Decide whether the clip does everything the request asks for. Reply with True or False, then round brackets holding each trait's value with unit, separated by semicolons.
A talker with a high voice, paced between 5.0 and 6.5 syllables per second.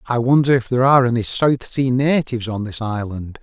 False (120 Hz; 5.7 syllables/s)